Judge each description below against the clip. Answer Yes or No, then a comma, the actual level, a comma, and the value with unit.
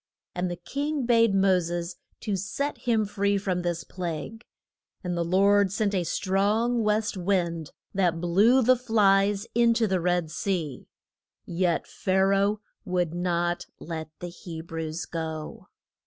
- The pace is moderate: Yes, average, 155 wpm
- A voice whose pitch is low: No, high, 190 Hz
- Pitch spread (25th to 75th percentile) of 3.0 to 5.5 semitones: Yes, average, 3.3 semitones